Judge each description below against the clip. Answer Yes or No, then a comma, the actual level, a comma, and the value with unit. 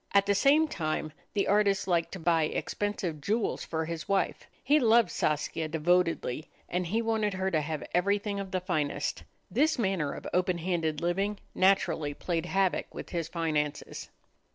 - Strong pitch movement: No, average, 3.8 semitones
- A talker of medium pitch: Yes, medium, 180 Hz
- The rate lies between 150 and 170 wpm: Yes, average, 165 wpm